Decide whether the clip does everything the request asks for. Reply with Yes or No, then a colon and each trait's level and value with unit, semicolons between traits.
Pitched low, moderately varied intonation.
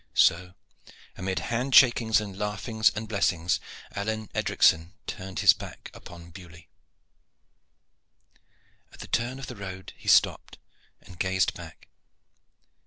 Yes: very low, 95 Hz; average, 3.7 semitones